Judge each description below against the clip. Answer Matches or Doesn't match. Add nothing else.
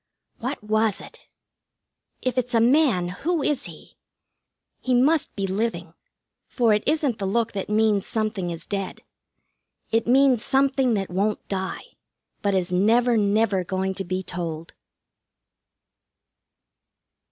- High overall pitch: Matches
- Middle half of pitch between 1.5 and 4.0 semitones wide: Doesn't match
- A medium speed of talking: Doesn't match